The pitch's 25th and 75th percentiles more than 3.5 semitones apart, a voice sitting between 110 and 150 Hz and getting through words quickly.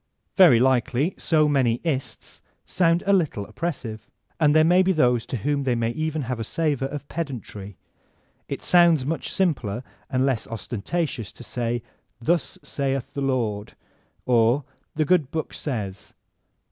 No: average, 5.1 semitones; low, 135 Hz; average, 150 wpm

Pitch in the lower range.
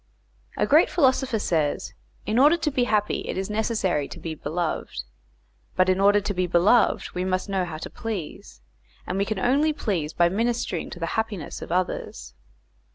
No: high, 195 Hz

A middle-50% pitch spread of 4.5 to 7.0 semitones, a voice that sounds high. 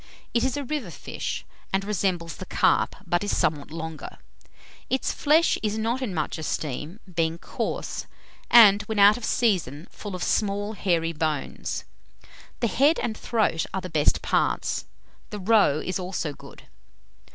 Yes: average, 5.2 semitones; high, 195 Hz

